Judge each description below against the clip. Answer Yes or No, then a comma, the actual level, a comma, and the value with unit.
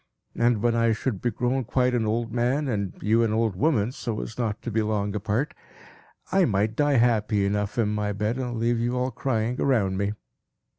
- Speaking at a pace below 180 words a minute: No, fast, 205 wpm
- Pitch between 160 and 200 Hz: No, low, 115 Hz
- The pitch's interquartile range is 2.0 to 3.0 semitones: Yes, average, 2.7 semitones